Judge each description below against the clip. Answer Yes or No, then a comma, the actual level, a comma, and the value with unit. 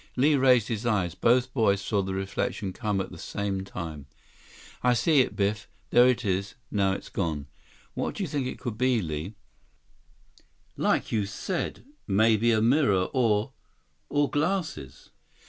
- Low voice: Yes, low, 105 Hz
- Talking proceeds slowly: No, average, 155 wpm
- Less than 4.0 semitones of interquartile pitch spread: No, average, 4.7 semitones